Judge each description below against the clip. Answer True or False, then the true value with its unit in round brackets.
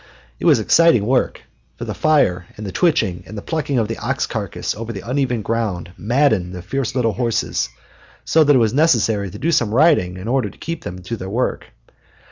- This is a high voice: False (115 Hz)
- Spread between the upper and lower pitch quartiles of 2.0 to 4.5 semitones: False (5.6 semitones)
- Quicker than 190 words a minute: True (205 wpm)